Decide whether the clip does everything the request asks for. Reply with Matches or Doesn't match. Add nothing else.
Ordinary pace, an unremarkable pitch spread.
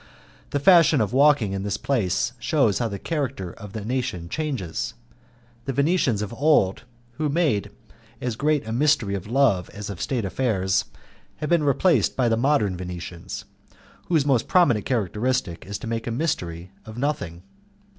Doesn't match